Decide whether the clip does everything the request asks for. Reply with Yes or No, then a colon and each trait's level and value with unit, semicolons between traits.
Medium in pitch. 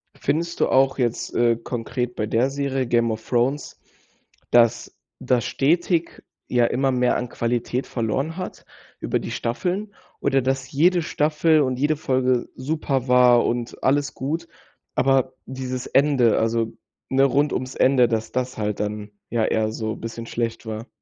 No: low, 130 Hz